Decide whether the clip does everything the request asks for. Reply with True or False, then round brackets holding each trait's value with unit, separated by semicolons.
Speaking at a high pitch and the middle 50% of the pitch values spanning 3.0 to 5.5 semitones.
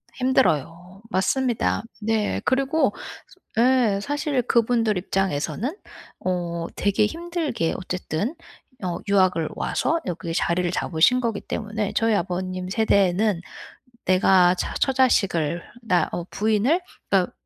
True (200 Hz; 5.1 semitones)